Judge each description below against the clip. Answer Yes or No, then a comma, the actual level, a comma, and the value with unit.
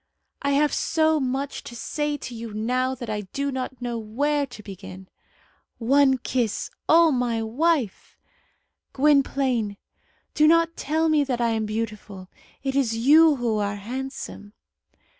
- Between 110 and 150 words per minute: Yes, average, 145 wpm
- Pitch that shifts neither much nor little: Yes, average, 4.4 semitones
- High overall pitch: Yes, very high, 255 Hz